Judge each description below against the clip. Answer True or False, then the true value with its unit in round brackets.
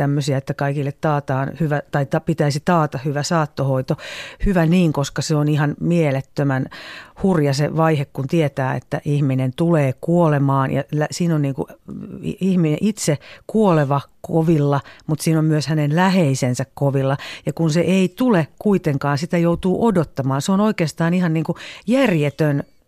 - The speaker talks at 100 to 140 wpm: False (150 wpm)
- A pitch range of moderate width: True (3.2 semitones)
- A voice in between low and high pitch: True (155 Hz)